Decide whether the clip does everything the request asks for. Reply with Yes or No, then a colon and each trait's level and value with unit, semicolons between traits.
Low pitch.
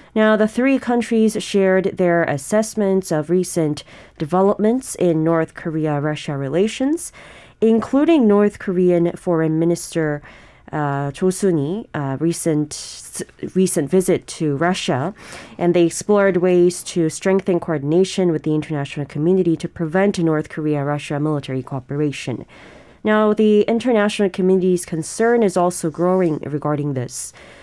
No: medium, 175 Hz